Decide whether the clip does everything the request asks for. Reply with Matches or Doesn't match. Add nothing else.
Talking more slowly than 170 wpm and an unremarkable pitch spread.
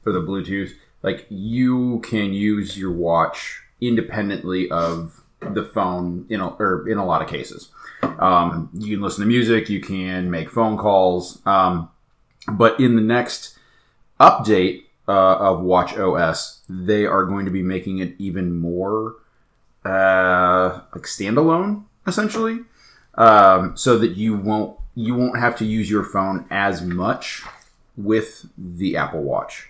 Matches